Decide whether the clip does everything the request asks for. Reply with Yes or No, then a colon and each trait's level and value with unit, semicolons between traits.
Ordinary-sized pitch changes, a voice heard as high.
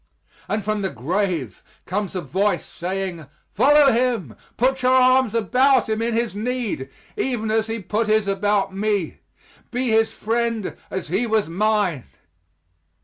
Yes: average, 3.5 semitones; high, 215 Hz